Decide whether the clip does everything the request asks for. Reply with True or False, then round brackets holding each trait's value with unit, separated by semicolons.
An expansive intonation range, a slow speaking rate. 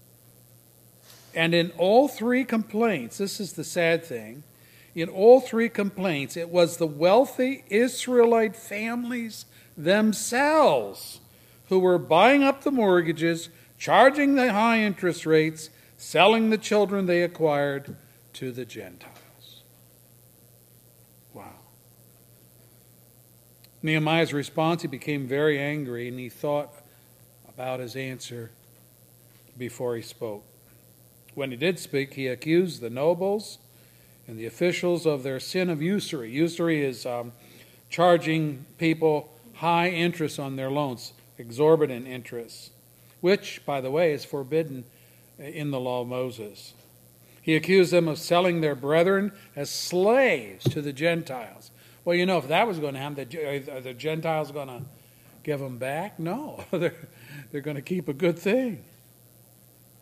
True (6.0 semitones; 130 wpm)